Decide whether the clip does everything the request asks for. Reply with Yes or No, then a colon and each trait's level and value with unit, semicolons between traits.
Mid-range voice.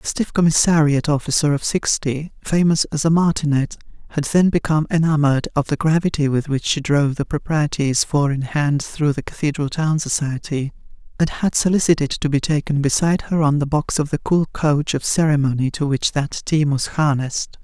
Yes: medium, 150 Hz